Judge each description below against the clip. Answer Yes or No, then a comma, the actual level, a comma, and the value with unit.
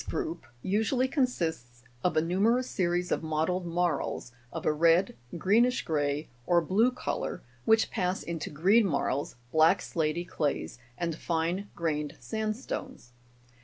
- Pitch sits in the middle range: Yes, medium, 175 Hz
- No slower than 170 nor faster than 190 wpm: No, slow, 135 wpm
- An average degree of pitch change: Yes, average, 4.8 semitones